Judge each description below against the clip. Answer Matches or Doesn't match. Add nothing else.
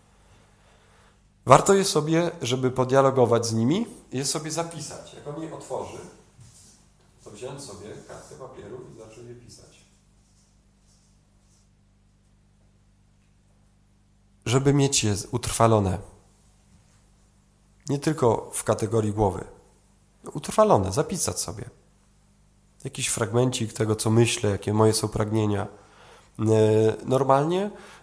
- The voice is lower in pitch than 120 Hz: Matches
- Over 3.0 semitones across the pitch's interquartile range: Matches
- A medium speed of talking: Doesn't match